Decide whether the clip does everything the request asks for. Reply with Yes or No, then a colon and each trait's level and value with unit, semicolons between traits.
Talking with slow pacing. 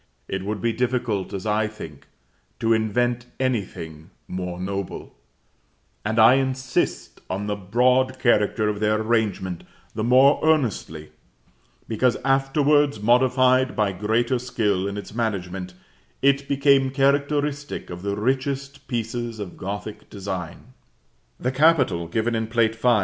Yes: slow, 130 wpm